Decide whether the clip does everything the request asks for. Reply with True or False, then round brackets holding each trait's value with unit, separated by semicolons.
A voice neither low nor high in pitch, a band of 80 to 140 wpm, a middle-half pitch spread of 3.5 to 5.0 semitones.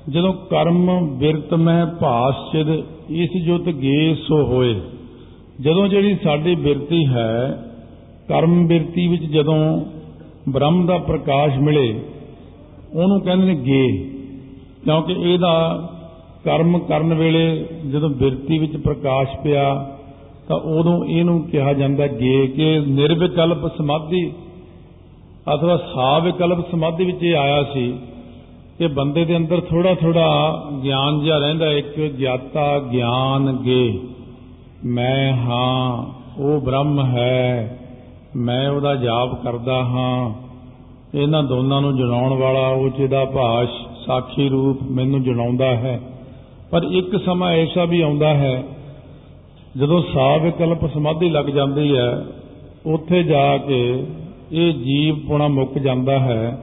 True (145 Hz; 115 wpm; 4.1 semitones)